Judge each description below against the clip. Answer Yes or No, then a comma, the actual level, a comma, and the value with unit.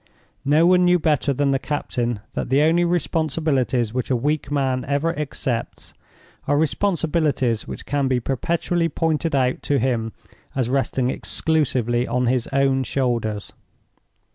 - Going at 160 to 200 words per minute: No, average, 140 wpm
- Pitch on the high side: No, low, 135 Hz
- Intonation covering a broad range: No, average, 3.9 semitones